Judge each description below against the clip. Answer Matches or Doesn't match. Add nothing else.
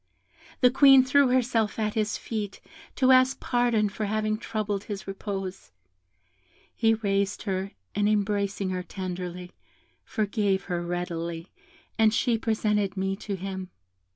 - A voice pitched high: Matches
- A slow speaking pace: Matches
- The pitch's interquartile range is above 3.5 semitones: Doesn't match